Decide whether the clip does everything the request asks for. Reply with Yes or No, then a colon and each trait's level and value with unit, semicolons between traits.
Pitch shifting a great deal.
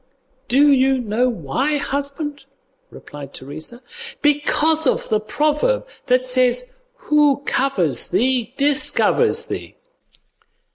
No: average, 3.5 semitones